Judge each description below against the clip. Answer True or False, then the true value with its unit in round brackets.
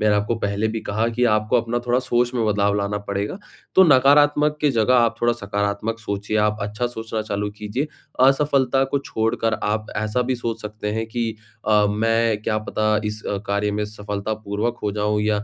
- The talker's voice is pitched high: False (110 Hz)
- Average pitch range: False (2.3 semitones)